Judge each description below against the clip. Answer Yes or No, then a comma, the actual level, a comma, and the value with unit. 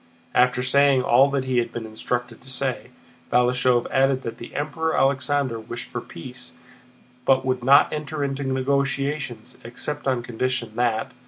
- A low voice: Yes, low, 130 Hz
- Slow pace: No, average, 150 wpm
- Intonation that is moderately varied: No, narrow, 2.1 semitones